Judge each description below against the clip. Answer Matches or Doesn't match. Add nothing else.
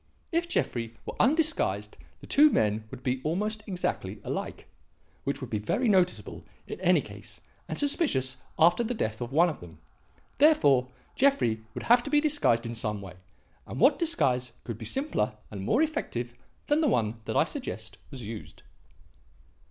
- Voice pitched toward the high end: Doesn't match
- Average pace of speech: Matches